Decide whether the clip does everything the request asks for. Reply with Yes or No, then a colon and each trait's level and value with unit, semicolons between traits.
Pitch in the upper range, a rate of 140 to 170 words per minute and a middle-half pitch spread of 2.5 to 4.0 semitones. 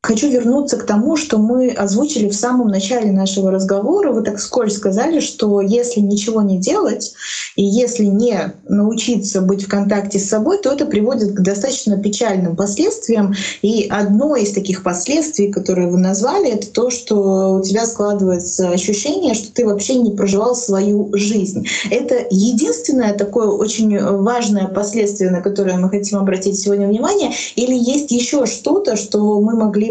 Yes: high, 210 Hz; fast, 160 wpm; average, 3.3 semitones